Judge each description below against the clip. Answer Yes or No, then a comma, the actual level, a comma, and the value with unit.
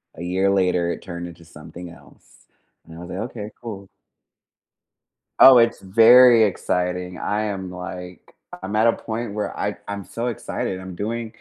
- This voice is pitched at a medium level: No, very low, 95 Hz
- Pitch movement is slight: No, average, 3.5 semitones